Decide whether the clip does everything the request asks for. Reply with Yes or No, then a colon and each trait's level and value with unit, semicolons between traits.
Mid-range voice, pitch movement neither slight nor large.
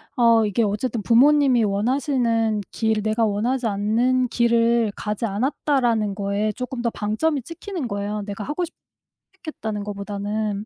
No: high, 225 Hz; average, 3.3 semitones